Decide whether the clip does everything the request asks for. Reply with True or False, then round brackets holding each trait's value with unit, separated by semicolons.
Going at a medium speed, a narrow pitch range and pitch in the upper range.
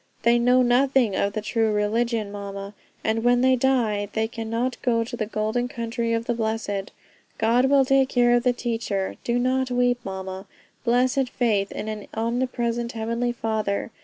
True (170 wpm; 2.2 semitones; 235 Hz)